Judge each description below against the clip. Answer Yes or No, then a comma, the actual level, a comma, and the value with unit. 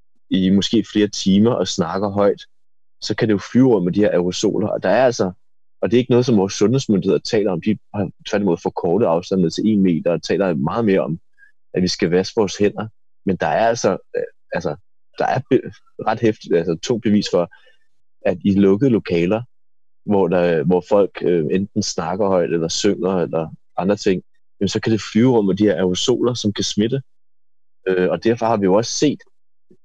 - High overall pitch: No, low, 100 Hz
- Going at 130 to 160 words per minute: No, average, 205 wpm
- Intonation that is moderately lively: Yes, average, 3.2 semitones